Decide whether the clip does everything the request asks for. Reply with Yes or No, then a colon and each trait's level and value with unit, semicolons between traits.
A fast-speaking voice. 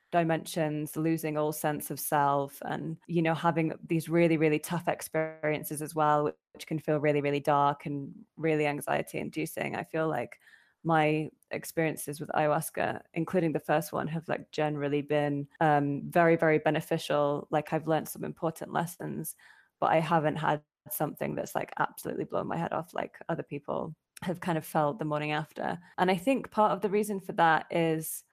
No: average, 180 wpm